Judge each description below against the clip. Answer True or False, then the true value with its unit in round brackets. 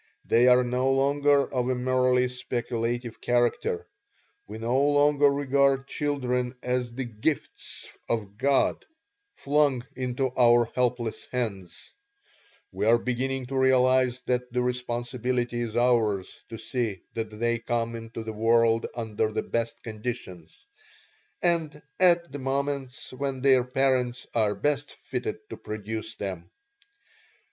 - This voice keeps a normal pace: False (130 wpm)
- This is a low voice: True (125 Hz)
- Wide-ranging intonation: False (2.4 semitones)